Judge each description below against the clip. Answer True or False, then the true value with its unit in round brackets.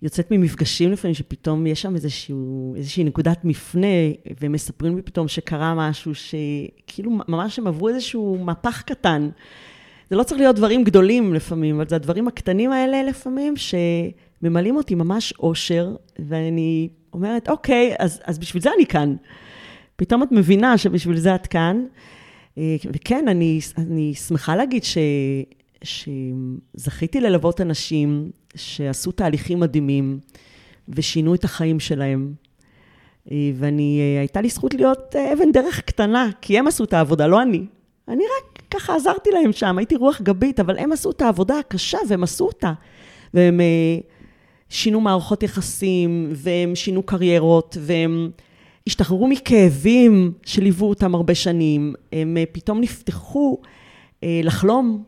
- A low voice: False (175 Hz)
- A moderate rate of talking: True (135 wpm)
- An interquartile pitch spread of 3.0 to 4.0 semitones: False (5.4 semitones)